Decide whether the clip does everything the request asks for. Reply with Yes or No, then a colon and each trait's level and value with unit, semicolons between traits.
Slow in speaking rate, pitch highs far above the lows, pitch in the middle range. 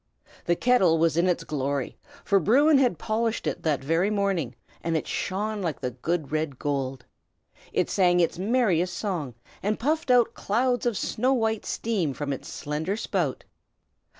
No: average, 165 wpm; wide, 6.3 semitones; medium, 180 Hz